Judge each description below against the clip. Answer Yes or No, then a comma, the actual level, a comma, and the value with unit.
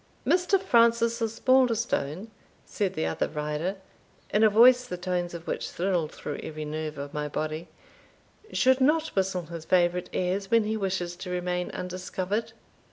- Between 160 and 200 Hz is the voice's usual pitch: Yes, medium, 185 Hz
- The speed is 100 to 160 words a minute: Yes, average, 155 wpm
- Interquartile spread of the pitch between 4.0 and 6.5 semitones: Yes, average, 5.2 semitones